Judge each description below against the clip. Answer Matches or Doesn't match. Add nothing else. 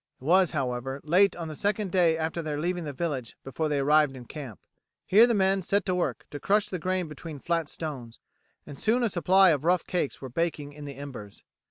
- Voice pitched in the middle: Matches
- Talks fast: Matches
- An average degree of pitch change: Matches